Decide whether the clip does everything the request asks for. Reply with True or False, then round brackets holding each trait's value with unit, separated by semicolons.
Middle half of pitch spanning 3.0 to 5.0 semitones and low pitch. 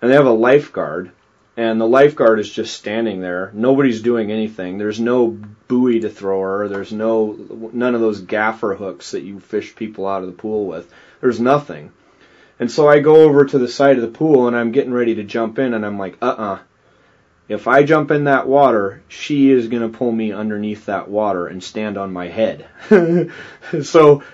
True (4.2 semitones; 115 Hz)